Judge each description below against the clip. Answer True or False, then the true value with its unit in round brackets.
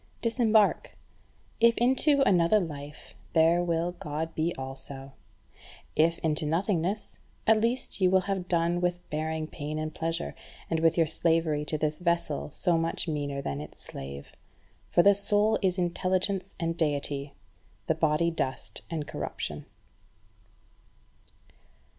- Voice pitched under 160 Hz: False (165 Hz)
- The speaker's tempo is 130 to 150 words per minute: True (135 wpm)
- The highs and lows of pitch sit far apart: False (3.3 semitones)